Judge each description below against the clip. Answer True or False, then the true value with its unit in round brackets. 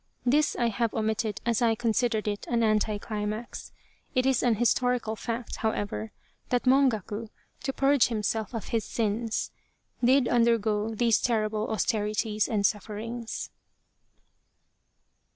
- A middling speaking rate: False (125 wpm)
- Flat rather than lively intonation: True (2.0 semitones)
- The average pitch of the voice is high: True (225 Hz)